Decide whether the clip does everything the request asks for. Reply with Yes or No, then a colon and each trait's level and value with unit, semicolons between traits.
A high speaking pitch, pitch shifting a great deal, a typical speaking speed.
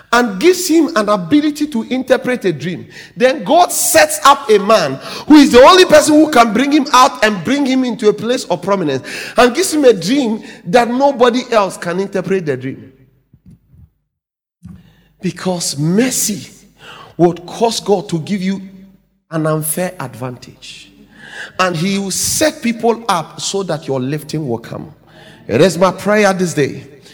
Yes: high, 205 Hz; wide, 6.6 semitones; average, 165 wpm